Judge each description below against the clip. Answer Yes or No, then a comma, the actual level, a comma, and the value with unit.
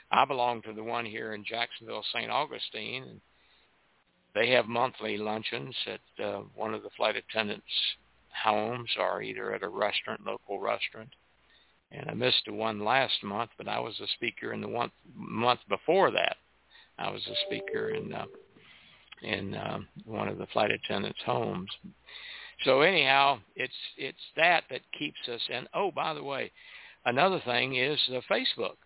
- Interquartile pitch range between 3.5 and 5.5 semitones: Yes, average, 4.8 semitones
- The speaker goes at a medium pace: Yes, average, 165 wpm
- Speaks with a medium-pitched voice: No, low, 120 Hz